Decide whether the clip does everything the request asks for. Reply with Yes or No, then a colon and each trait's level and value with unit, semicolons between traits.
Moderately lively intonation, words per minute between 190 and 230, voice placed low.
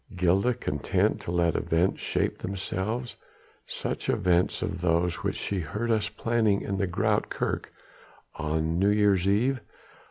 No: average, 3.5 semitones; average, 140 wpm; very low, 95 Hz